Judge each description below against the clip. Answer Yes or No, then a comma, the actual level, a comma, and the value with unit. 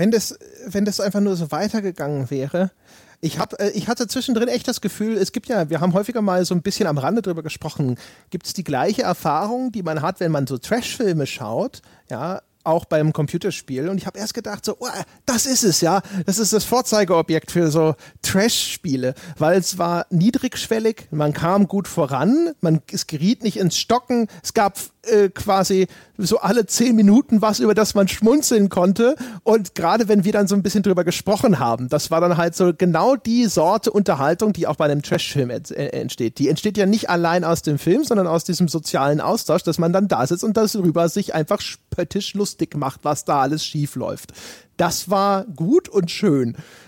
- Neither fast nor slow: No, fast, 200 wpm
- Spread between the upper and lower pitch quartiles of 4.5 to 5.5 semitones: Yes, average, 4.9 semitones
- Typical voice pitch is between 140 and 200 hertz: Yes, high, 190 Hz